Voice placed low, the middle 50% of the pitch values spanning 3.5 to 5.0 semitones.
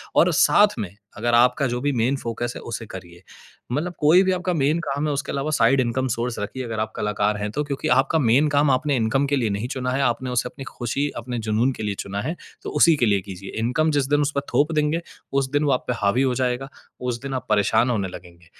Yes: low, 125 Hz; average, 4.2 semitones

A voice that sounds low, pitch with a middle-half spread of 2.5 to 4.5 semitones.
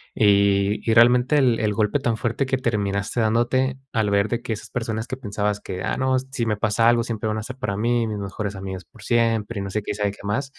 Yes: low, 110 Hz; average, 2.8 semitones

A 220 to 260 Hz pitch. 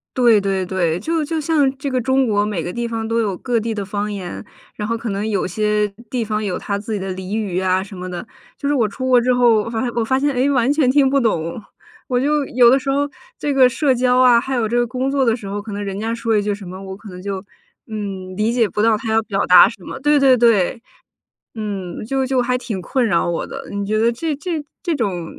Yes: high, 225 Hz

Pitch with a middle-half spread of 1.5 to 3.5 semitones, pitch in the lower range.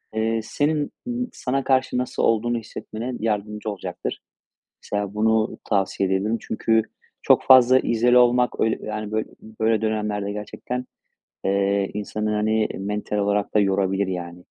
Yes: average, 2.7 semitones; low, 110 Hz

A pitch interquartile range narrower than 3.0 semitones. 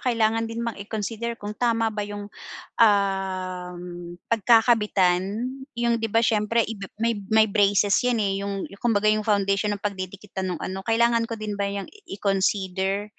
Yes: narrow, 2.5 semitones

